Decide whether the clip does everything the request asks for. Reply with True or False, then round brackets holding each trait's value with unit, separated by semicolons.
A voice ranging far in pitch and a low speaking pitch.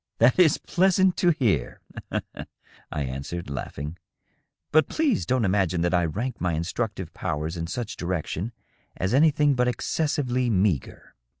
True (7.9 semitones; 105 Hz)